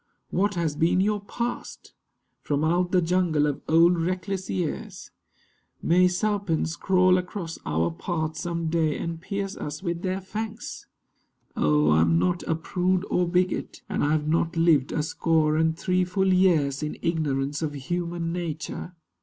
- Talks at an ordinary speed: Yes, average, 160 wpm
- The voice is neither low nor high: Yes, medium, 170 Hz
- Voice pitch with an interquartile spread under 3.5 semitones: Yes, average, 2.8 semitones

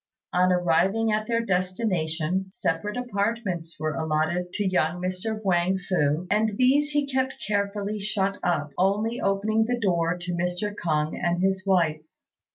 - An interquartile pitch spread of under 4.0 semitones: Yes, average, 3.5 semitones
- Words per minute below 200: Yes, average, 150 wpm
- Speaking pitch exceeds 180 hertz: Yes, high, 190 Hz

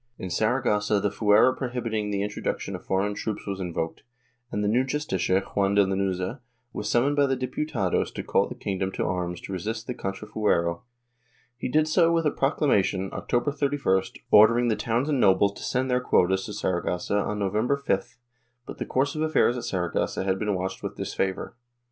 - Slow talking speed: No, average, 190 wpm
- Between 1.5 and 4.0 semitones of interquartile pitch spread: No, average, 4.8 semitones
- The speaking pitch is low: Yes, low, 105 Hz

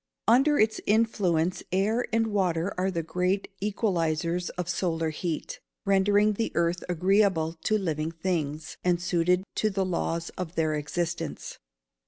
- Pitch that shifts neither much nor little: Yes, average, 3.5 semitones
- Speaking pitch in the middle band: Yes, medium, 180 Hz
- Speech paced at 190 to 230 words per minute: No, average, 145 wpm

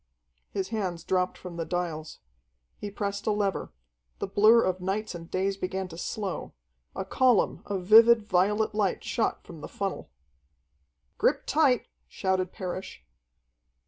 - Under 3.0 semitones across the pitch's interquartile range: Yes, narrow, 2.4 semitones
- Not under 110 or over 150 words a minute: Yes, average, 145 wpm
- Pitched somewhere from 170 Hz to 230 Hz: Yes, high, 190 Hz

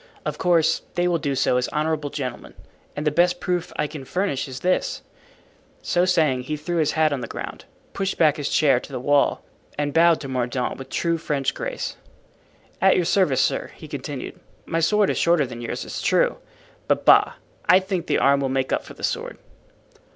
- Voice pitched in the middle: Yes, medium, 155 Hz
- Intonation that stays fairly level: No, average, 4.4 semitones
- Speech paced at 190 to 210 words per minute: Yes, average, 200 wpm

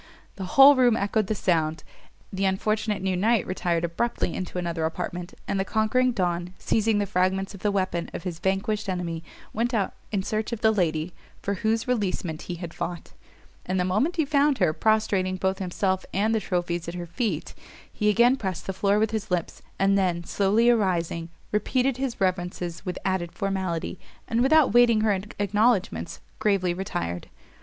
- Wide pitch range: No, average, 3.6 semitones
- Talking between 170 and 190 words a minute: Yes, average, 180 wpm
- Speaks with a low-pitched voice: No, high, 195 Hz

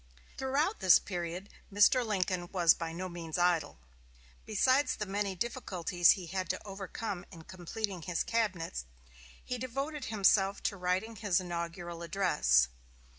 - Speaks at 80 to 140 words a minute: Yes, slow, 135 wpm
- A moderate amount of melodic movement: Yes, average, 3.7 semitones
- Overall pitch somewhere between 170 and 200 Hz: Yes, medium, 185 Hz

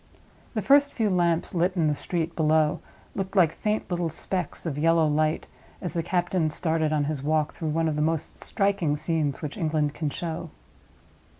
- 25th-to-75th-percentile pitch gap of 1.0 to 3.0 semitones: Yes, narrow, 2.5 semitones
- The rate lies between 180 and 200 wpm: Yes, average, 185 wpm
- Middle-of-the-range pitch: Yes, medium, 165 Hz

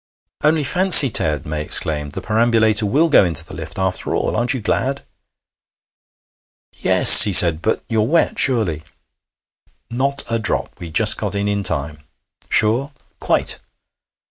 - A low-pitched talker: Yes, low, 105 Hz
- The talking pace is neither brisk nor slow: Yes, average, 145 wpm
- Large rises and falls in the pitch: Yes, wide, 7.1 semitones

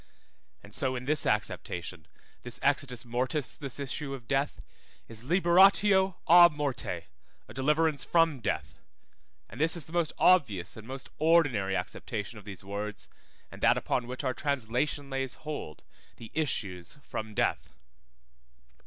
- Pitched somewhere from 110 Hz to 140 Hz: Yes, low, 135 Hz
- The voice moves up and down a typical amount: No, wide, 5.8 semitones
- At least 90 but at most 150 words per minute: Yes, average, 145 wpm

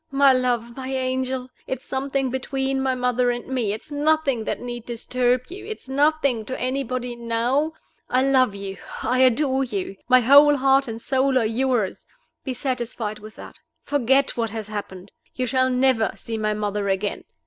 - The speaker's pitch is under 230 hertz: No, very high, 255 Hz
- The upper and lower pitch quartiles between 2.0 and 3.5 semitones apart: Yes, narrow, 2.6 semitones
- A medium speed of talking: Yes, average, 170 wpm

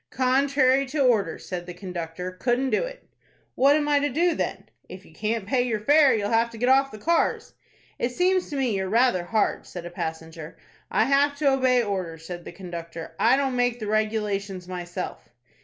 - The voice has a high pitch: Yes, high, 225 Hz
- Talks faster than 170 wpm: Yes, average, 200 wpm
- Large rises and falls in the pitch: Yes, wide, 6.7 semitones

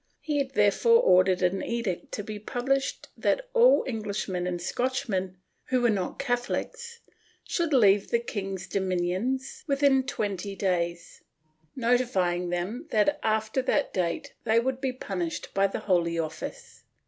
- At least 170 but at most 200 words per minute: No, average, 145 wpm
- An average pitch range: No, wide, 6.0 semitones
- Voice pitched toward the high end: Yes, high, 215 Hz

